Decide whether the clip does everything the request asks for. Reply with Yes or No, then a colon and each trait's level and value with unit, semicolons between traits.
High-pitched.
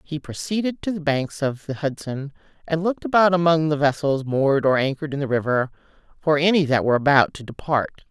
No: medium, 150 Hz